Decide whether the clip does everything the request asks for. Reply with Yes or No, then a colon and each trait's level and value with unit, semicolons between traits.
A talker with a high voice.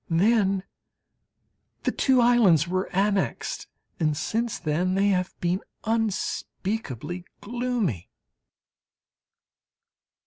Yes: high, 195 Hz